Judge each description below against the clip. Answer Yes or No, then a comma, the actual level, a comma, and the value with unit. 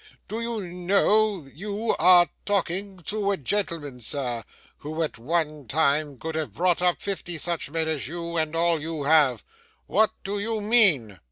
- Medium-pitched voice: Yes, medium, 170 Hz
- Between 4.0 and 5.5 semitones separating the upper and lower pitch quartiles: Yes, average, 4.9 semitones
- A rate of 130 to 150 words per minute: No, average, 170 wpm